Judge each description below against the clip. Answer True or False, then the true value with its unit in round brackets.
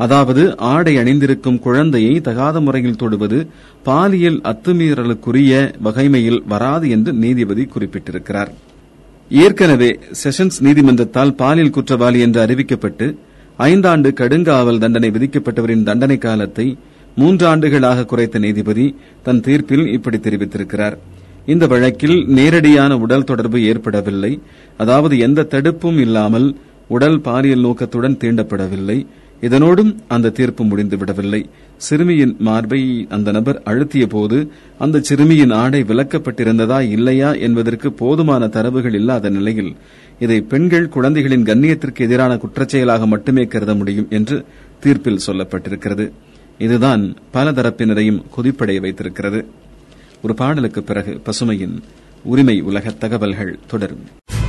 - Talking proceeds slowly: False (95 wpm)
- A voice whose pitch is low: True (125 Hz)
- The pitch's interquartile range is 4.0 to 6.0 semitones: True (4.4 semitones)